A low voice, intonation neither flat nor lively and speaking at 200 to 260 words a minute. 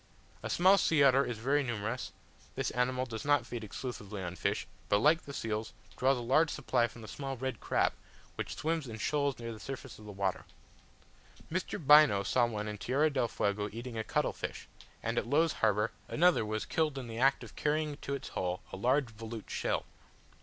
Yes: low, 125 Hz; average, 4.7 semitones; fast, 205 wpm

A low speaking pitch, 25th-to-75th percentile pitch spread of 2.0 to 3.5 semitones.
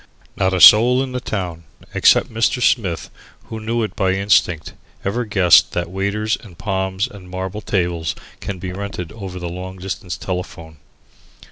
Yes: very low, 95 Hz; average, 3.0 semitones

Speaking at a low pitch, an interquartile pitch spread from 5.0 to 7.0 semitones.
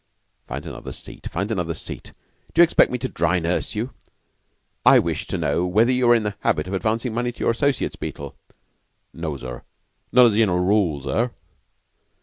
Yes: low, 105 Hz; wide, 5.6 semitones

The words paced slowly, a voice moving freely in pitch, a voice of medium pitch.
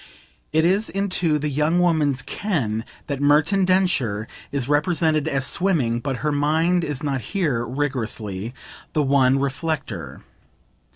No: slow, 130 wpm; average, 4.1 semitones; medium, 145 Hz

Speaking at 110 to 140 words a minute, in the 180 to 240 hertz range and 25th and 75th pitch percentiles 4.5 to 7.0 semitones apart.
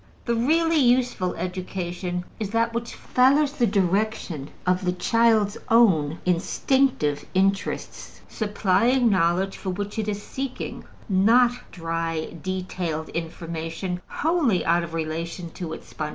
Yes: slow, 135 wpm; high, 190 Hz; average, 5.3 semitones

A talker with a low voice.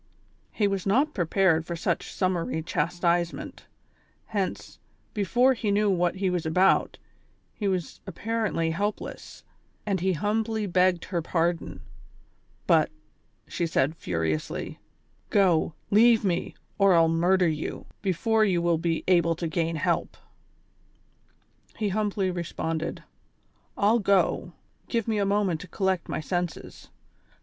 No: medium, 185 Hz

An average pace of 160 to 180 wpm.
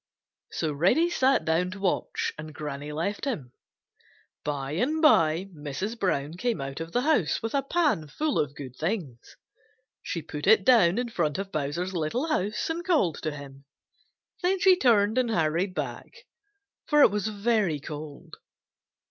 Yes: average, 165 wpm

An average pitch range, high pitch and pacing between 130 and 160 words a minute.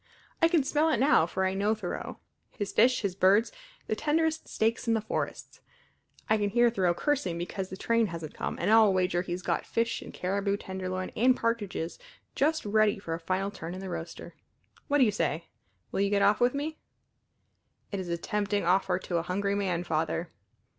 No: average, 4.0 semitones; high, 200 Hz; average, 200 wpm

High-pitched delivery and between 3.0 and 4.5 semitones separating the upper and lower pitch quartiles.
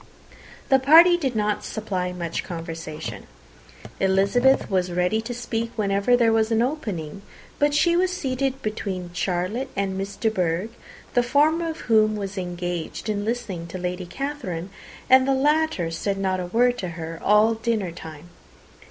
No: high, 210 Hz; wide, 5.6 semitones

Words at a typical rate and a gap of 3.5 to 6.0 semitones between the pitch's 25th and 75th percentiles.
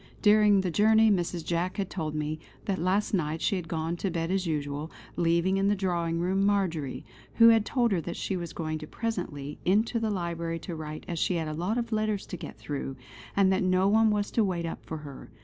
No: fast, 225 wpm; average, 3.8 semitones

